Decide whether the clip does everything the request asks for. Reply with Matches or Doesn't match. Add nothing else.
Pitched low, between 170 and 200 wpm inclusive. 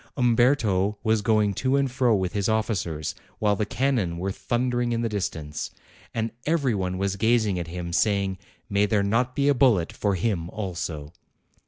Matches